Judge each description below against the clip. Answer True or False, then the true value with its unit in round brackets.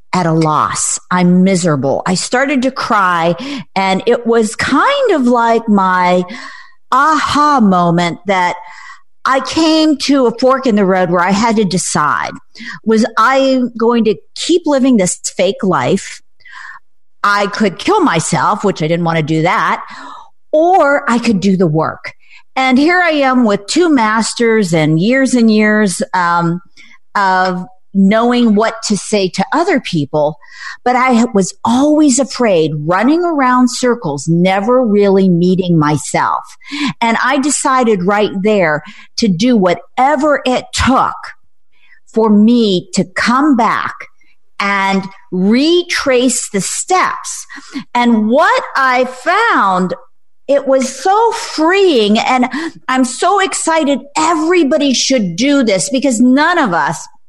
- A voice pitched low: False (235 Hz)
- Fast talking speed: False (135 wpm)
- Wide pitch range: True (6.2 semitones)